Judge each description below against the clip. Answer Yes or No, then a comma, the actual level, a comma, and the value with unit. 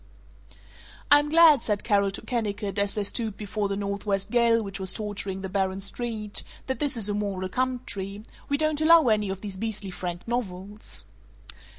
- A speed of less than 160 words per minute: No, average, 175 wpm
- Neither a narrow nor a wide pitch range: Yes, average, 3.3 semitones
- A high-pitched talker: Yes, high, 210 Hz